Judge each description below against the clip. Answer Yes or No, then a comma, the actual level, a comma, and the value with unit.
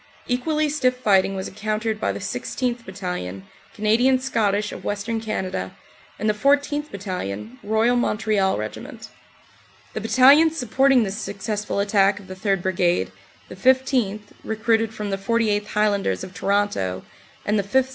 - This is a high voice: Yes, high, 210 Hz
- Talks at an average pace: Yes, average, 145 wpm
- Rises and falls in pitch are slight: No, average, 3.9 semitones